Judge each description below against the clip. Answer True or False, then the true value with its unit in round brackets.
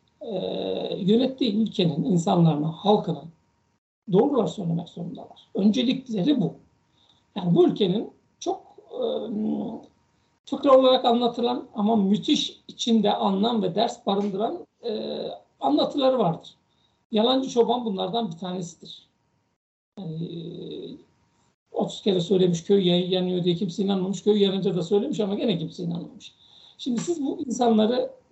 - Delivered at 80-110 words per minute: False (120 wpm)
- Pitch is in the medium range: False (205 Hz)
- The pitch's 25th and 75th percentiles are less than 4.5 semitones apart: False (5.2 semitones)